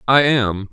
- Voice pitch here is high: No, low, 120 Hz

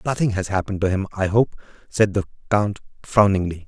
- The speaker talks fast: No, average, 180 wpm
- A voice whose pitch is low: Yes, low, 100 Hz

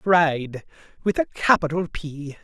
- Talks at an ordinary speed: No, slow, 100 wpm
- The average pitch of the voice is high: No, medium, 160 Hz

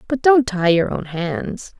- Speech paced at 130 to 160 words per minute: No, average, 200 wpm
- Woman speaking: Yes, female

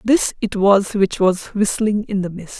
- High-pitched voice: Yes, high, 200 Hz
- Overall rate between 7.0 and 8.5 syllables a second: No, 4.1 syllables/s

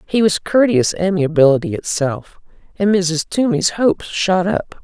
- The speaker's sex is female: Yes, female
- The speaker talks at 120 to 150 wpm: Yes, slow, 135 wpm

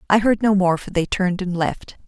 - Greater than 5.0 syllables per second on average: Yes, 5.5 syllables/s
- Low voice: No, high, 190 Hz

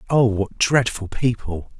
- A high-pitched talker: No, low, 110 Hz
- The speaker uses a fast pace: No, slow, 135 wpm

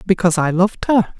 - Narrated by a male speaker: No, female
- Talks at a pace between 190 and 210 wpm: Yes, average, 200 wpm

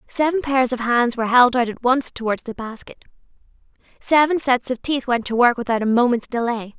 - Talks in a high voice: Yes, high, 245 Hz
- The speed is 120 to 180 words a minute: No, fast, 205 wpm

